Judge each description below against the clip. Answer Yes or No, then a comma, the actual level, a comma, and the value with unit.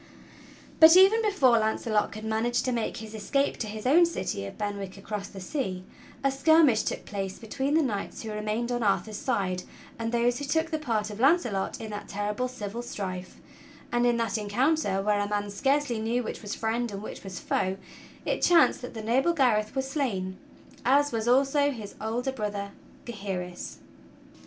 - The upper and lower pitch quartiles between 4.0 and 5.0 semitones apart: Yes, average, 4.5 semitones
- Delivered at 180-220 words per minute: Yes, average, 185 wpm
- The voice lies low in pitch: No, high, 225 Hz